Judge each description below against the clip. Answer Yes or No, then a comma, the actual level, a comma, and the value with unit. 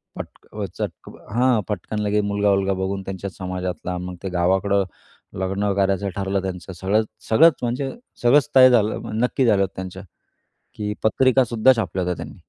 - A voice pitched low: Yes, low, 100 Hz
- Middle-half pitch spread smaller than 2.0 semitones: No, average, 2.9 semitones